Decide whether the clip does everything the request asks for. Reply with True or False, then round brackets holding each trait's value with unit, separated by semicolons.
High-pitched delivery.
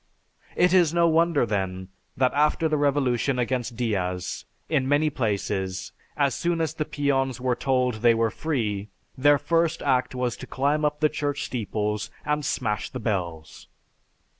False (130 Hz)